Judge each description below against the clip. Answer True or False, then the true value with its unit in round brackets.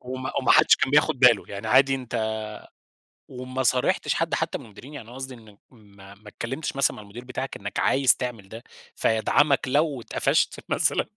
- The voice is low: True (125 Hz)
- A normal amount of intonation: True (3.4 semitones)